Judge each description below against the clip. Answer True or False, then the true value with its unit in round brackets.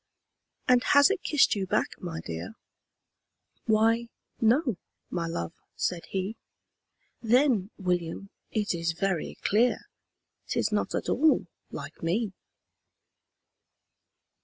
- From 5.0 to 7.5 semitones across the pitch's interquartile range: True (5.3 semitones)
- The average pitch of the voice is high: True (205 Hz)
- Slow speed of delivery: True (110 wpm)